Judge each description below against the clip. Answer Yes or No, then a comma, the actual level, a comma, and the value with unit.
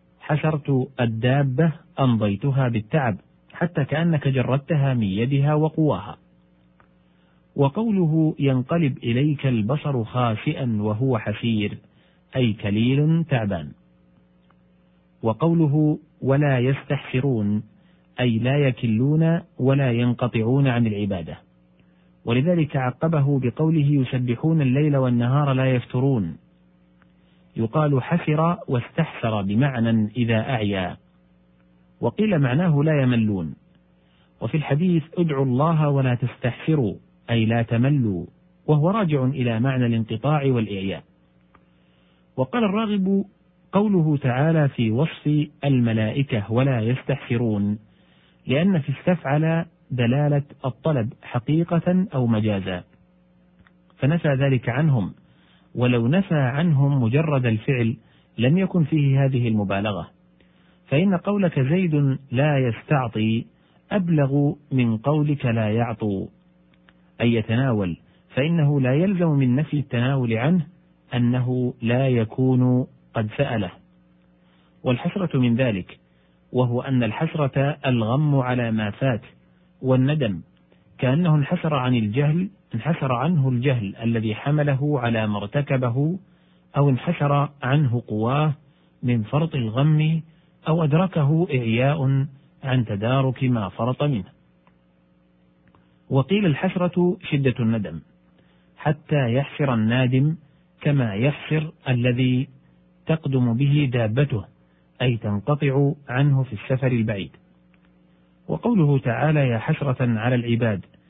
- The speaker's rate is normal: Yes, average, 95 wpm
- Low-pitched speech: Yes, low, 130 Hz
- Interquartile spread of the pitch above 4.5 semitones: Yes, wide, 5.4 semitones